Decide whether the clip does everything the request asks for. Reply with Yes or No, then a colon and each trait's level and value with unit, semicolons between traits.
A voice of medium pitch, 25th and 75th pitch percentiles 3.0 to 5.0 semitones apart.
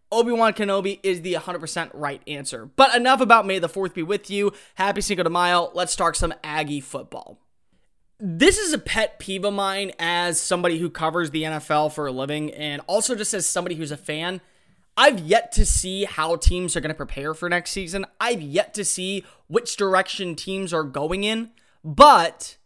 Yes: medium, 180 Hz; average, 4.1 semitones